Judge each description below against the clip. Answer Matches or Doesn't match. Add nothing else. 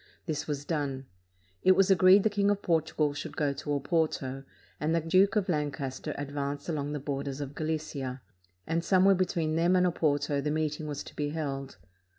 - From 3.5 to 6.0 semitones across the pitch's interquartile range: Doesn't match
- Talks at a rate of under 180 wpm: Doesn't match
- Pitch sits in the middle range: Matches